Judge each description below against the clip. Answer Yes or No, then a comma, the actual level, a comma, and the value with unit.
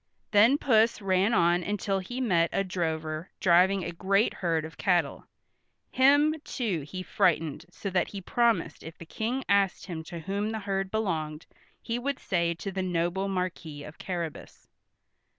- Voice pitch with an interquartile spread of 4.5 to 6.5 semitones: No, average, 3.7 semitones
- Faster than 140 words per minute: Yes, average, 165 wpm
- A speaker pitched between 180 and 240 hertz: Yes, medium, 185 Hz